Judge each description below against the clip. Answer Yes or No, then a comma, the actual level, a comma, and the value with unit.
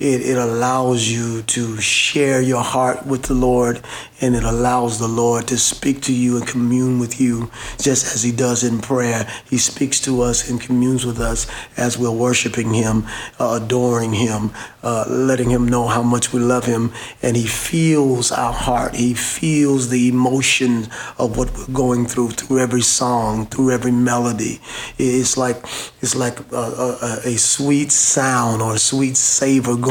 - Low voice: Yes, low, 125 Hz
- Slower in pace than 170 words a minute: No, average, 175 wpm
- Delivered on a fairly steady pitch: Yes, narrow, 1.4 semitones